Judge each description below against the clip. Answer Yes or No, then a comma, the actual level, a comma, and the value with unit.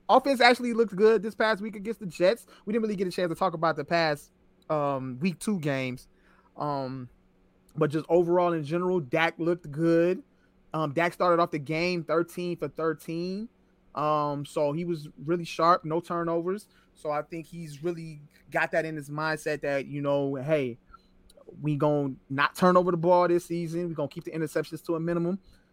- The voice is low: No, medium, 165 Hz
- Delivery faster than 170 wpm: Yes, average, 195 wpm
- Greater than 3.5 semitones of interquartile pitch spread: No, average, 3.2 semitones